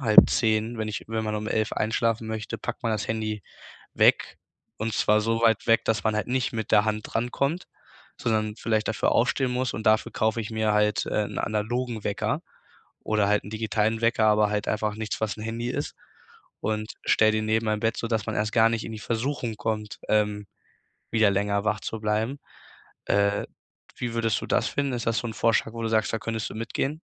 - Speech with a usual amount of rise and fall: No, narrow, 1.2 semitones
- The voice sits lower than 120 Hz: Yes, low, 110 Hz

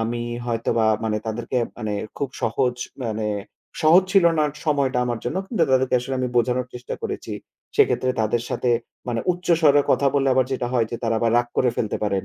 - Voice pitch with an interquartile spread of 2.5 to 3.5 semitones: Yes, average, 2.8 semitones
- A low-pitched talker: Yes, low, 125 Hz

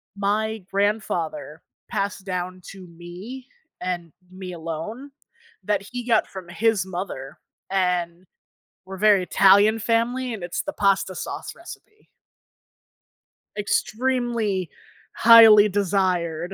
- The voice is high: Yes, high, 195 Hz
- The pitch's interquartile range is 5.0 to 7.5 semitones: No, average, 3.4 semitones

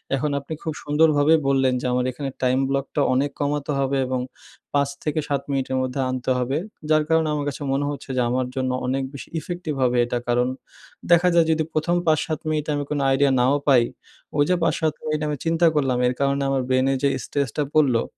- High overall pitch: No, medium, 140 Hz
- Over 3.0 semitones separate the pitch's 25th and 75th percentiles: No, average, 2.7 semitones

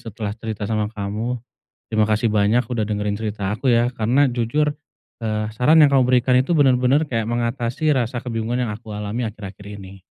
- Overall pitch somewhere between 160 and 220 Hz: No, low, 115 Hz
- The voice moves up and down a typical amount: Yes, average, 3.0 semitones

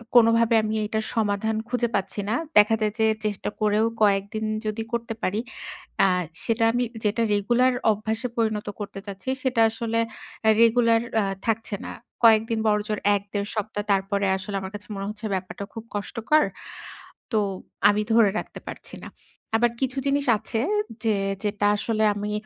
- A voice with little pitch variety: Yes, narrow, 1.8 semitones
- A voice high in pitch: Yes, high, 215 Hz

